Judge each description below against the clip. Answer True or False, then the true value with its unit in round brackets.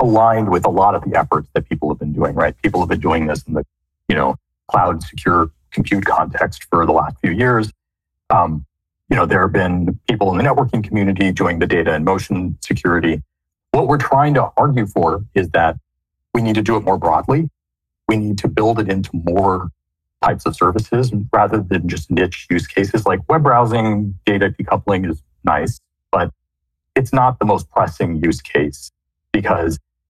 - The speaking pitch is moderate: False (95 Hz)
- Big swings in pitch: True (5.8 semitones)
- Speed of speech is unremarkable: True (190 wpm)